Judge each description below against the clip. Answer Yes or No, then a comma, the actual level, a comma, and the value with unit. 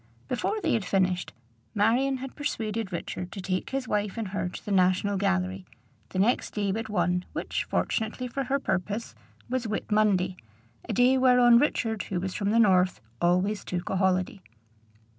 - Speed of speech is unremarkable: Yes, average, 175 wpm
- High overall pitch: Yes, high, 205 Hz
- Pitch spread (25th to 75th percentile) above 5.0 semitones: No, average, 4.1 semitones